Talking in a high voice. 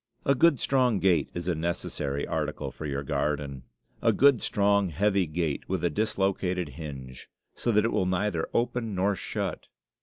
No: very low, 90 Hz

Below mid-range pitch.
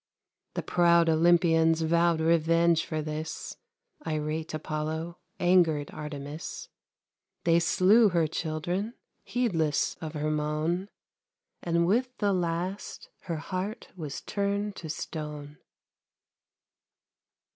No: medium, 165 Hz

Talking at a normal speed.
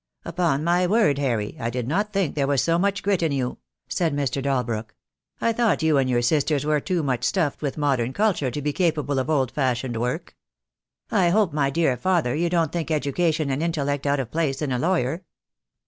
No: fast, 210 wpm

